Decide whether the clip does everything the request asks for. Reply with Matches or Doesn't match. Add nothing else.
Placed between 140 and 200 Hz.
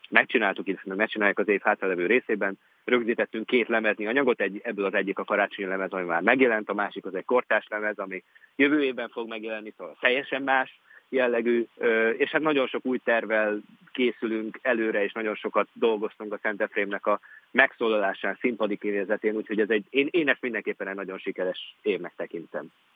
Doesn't match